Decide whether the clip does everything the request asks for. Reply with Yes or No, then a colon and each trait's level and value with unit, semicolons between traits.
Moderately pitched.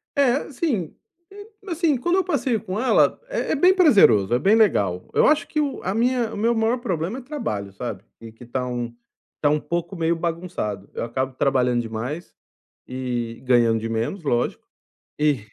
Yes: medium, 170 Hz